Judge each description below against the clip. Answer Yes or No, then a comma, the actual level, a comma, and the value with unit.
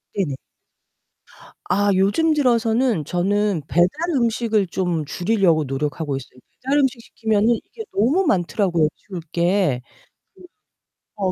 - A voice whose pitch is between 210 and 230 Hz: No, high, 200 Hz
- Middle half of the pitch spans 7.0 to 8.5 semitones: No, average, 5.2 semitones